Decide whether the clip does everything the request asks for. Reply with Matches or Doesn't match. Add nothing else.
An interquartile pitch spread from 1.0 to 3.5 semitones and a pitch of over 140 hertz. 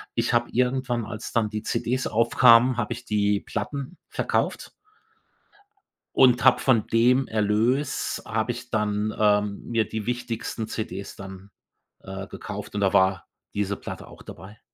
Doesn't match